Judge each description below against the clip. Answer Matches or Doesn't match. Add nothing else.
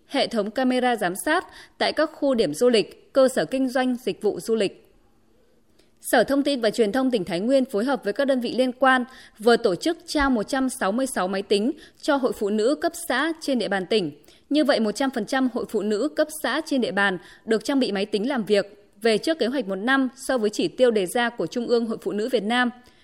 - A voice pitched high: Matches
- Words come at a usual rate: Matches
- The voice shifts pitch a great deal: Doesn't match